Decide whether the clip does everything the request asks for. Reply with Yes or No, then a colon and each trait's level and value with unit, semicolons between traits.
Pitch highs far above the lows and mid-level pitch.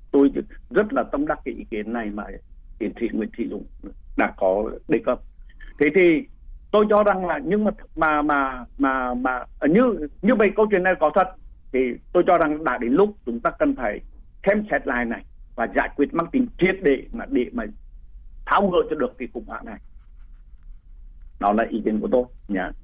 Yes: wide, 8.9 semitones; medium, 155 Hz